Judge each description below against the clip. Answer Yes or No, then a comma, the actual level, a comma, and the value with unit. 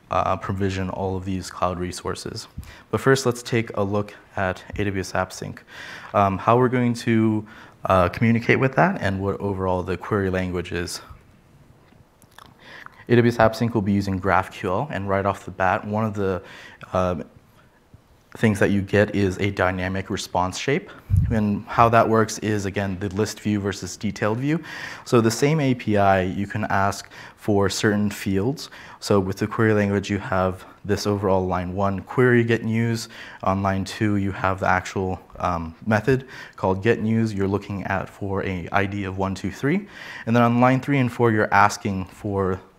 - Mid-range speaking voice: No, low, 100 Hz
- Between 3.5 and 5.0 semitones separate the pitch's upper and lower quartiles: No, average, 2.9 semitones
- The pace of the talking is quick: No, average, 175 wpm